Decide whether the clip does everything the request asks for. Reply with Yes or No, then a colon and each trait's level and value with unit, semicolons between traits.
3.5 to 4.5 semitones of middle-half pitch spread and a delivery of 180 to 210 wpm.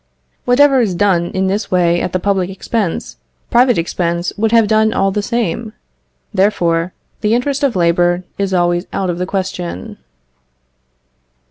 No: average, 3.8 semitones; average, 150 wpm